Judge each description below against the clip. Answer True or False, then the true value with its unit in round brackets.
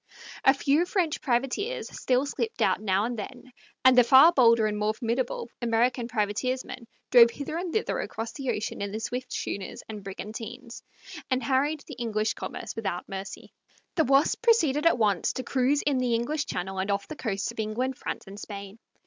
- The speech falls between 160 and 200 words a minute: True (185 wpm)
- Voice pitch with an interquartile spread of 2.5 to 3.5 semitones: False (4.2 semitones)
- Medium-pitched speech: False (240 Hz)